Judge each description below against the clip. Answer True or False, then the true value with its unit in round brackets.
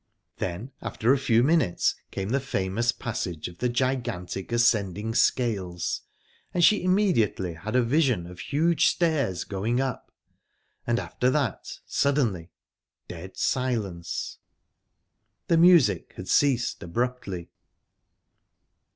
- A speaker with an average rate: False (110 wpm)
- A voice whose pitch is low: True (120 Hz)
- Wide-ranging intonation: True (6.3 semitones)